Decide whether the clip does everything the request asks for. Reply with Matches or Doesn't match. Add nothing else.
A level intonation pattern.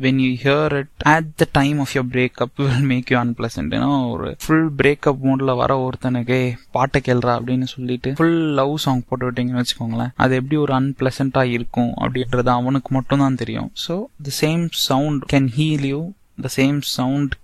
Matches